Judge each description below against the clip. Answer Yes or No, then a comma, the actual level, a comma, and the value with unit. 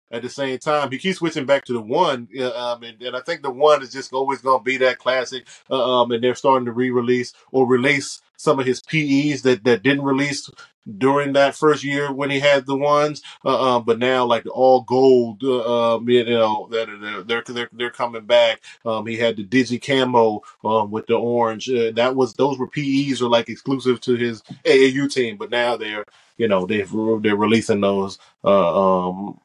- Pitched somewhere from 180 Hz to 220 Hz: No, low, 125 Hz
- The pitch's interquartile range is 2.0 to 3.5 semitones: Yes, average, 2.7 semitones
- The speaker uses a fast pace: Yes, fast, 210 wpm